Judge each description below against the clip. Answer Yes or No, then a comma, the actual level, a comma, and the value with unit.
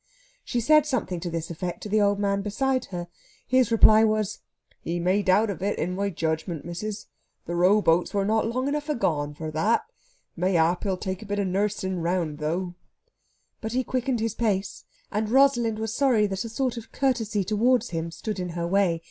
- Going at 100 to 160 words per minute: No, average, 195 wpm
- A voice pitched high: Yes, high, 200 Hz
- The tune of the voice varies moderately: Yes, average, 4.3 semitones